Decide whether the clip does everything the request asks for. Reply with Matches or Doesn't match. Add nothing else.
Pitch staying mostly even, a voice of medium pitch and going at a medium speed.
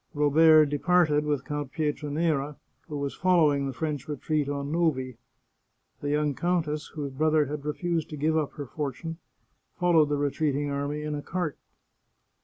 Matches